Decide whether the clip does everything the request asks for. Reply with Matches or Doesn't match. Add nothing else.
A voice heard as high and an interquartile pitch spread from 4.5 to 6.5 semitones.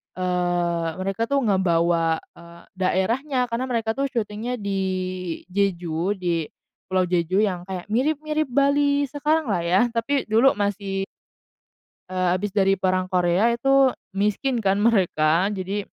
Matches